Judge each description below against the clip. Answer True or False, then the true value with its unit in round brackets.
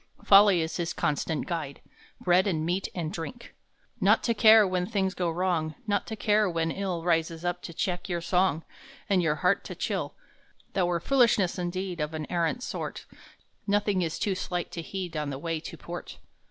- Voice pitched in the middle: True (180 Hz)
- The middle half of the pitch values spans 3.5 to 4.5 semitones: False (3.0 semitones)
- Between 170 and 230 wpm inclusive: True (190 wpm)